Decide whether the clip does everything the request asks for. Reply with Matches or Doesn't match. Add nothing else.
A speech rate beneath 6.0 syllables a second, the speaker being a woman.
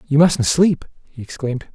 Doesn't match